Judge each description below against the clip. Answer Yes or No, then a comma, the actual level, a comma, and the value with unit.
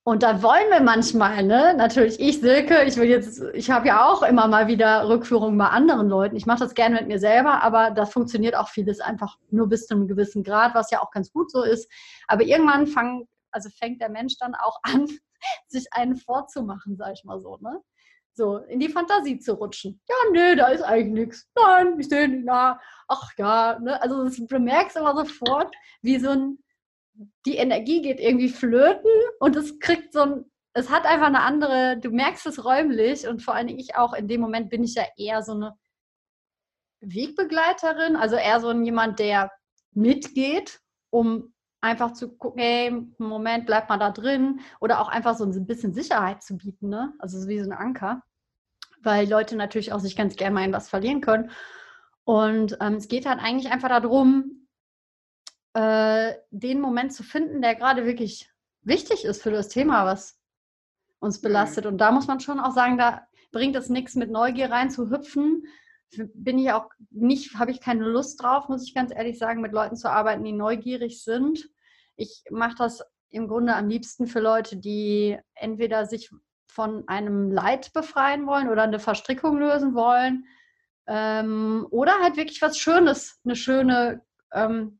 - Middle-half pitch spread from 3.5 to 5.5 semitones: Yes, average, 3.9 semitones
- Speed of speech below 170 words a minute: No, fast, 190 wpm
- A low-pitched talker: No, high, 240 Hz